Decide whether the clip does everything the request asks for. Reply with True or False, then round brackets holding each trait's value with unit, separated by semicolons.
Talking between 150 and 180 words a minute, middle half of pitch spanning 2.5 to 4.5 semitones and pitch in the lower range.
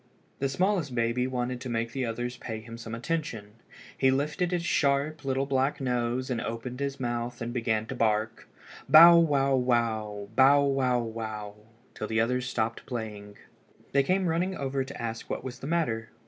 True (170 wpm; 3.3 semitones; 125 Hz)